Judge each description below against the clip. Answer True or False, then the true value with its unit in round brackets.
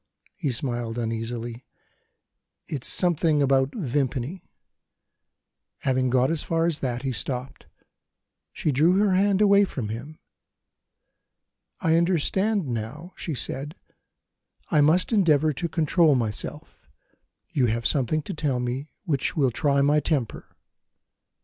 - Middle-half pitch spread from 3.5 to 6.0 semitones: True (4.8 semitones)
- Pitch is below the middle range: False (145 Hz)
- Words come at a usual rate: False (125 wpm)